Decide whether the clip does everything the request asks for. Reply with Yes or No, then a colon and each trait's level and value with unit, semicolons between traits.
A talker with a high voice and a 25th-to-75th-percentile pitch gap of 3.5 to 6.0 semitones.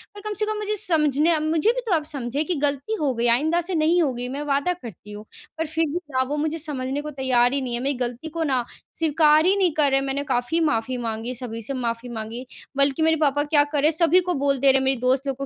Yes: very high, 285 Hz; average, 4.0 semitones